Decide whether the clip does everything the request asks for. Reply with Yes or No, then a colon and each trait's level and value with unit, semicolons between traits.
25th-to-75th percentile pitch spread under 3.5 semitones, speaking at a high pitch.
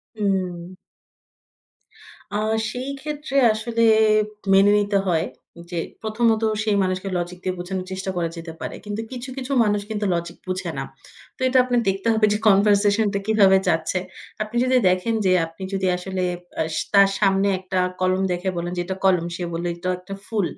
Yes: average, 2.9 semitones; high, 195 Hz